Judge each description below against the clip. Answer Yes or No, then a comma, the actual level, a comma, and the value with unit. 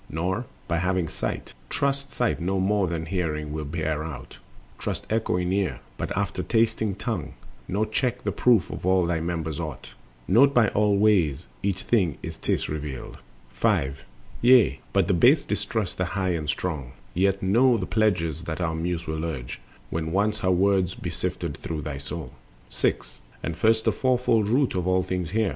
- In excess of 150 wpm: Yes, average, 180 wpm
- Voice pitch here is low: Yes, very low, 90 Hz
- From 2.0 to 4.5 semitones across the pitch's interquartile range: No, average, 5.0 semitones